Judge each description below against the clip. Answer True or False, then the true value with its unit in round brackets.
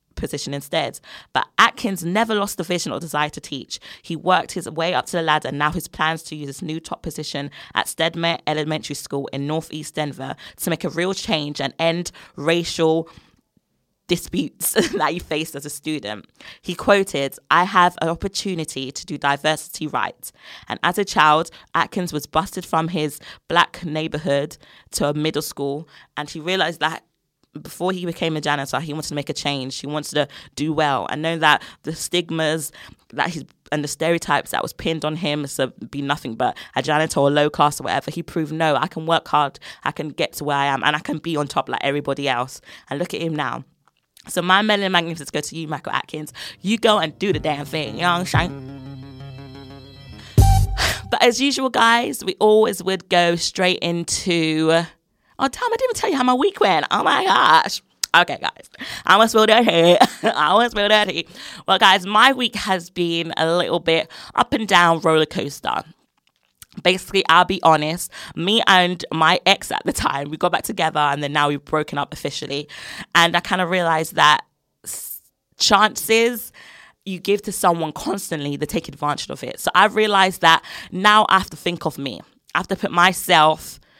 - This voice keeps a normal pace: True (195 wpm)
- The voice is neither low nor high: True (160 Hz)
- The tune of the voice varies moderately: True (3.8 semitones)